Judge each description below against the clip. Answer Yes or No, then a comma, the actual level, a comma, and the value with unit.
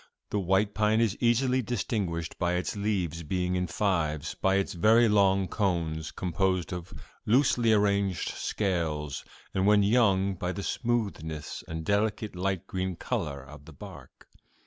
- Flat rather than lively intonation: No, average, 3.8 semitones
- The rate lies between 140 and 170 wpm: Yes, average, 145 wpm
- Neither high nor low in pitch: No, very low, 95 Hz